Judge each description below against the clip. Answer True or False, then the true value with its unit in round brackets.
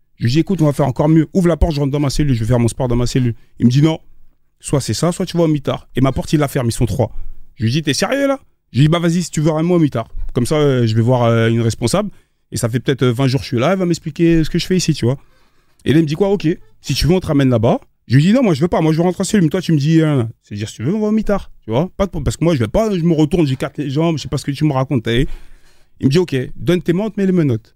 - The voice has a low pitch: False (150 Hz)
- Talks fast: True (360 wpm)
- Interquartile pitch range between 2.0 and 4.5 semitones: False (5.3 semitones)